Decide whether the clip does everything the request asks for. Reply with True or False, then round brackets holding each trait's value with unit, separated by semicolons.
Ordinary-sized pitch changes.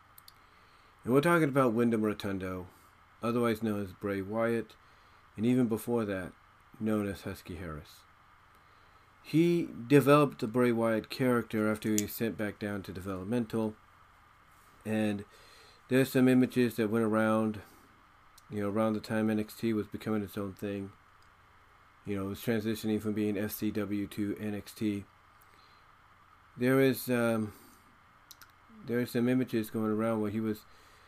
False (2.3 semitones)